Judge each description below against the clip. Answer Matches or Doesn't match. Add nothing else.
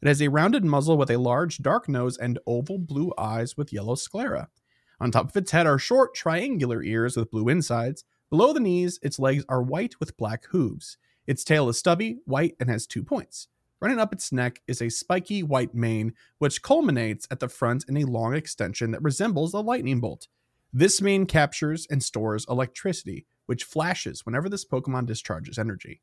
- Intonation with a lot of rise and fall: Matches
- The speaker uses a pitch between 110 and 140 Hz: Matches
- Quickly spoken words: Doesn't match